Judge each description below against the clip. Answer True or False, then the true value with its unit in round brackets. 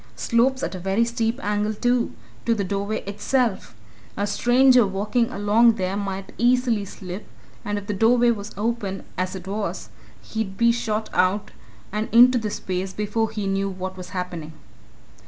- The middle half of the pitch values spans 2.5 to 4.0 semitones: True (3.1 semitones)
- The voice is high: True (210 Hz)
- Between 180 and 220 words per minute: False (160 wpm)